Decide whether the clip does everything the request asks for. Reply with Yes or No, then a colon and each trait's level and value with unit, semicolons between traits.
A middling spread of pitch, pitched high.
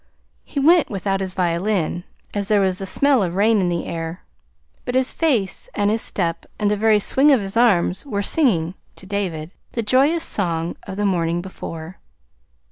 Yes: average, 4.5 semitones; high, 200 Hz